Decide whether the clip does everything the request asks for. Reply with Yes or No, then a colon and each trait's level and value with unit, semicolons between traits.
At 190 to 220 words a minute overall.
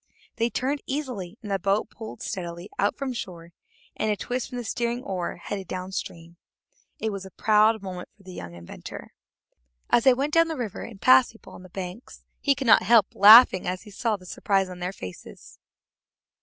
Yes: fast, 205 wpm